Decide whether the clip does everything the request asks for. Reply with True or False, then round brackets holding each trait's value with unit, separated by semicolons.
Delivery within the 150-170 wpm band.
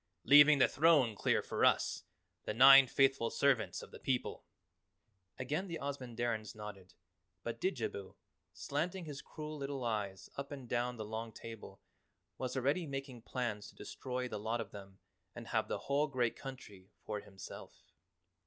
True (155 wpm)